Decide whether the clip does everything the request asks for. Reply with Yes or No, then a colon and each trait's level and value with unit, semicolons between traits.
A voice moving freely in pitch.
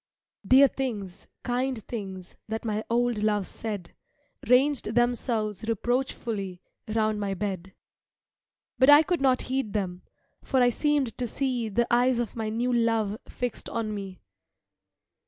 No: average, 3.2 semitones